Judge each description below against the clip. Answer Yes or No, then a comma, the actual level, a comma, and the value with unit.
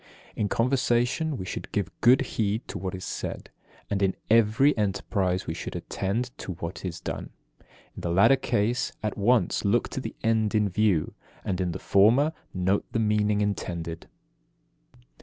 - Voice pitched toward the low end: Yes, low, 105 Hz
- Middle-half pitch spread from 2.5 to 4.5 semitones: Yes, average, 4.0 semitones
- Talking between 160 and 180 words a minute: Yes, average, 170 wpm